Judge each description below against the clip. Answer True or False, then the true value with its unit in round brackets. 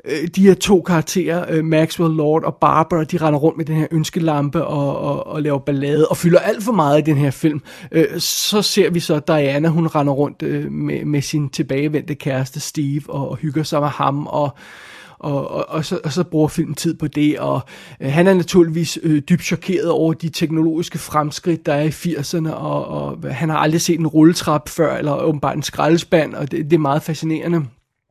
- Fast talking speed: False (200 wpm)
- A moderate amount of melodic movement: False (2.3 semitones)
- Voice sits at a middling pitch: True (155 Hz)